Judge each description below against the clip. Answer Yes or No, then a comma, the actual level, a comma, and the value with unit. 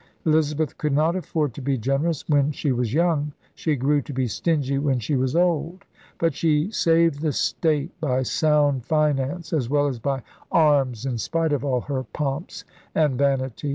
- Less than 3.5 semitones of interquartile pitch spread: Yes, average, 2.9 semitones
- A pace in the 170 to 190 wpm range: Yes, average, 180 wpm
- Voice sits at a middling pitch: Yes, medium, 145 Hz